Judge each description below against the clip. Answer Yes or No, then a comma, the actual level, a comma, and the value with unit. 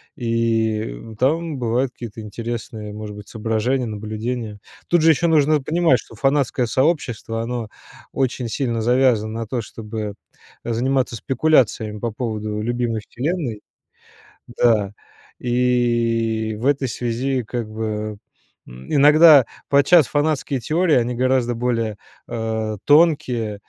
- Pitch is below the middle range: Yes, low, 120 Hz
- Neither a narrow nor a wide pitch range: Yes, average, 3.3 semitones